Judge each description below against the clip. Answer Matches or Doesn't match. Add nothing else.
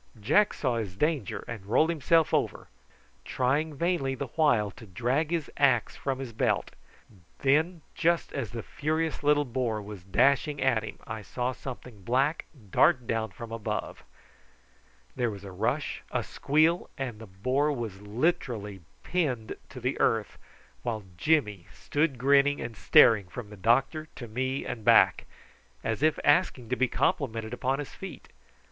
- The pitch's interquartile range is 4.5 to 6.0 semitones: Matches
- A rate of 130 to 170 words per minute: Matches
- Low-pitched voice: Matches